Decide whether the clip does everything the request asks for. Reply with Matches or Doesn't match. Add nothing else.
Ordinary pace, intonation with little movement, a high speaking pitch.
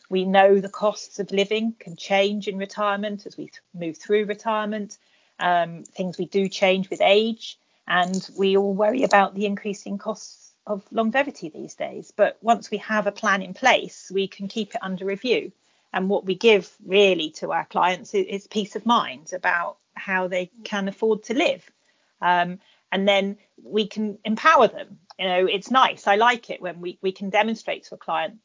Matches